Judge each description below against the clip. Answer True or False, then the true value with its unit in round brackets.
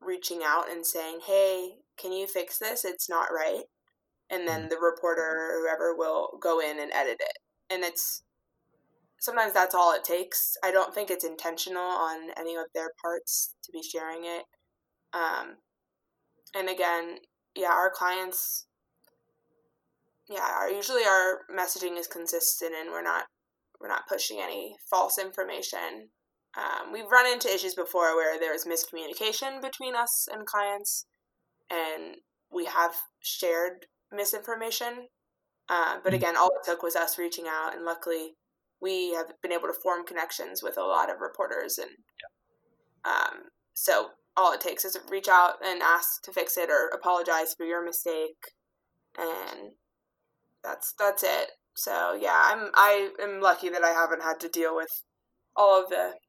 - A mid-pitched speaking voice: True (180 Hz)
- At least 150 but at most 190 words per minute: True (160 wpm)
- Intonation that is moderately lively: True (3.4 semitones)